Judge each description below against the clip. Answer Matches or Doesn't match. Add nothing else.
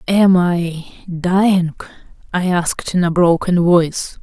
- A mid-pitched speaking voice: Matches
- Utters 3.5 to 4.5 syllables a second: Matches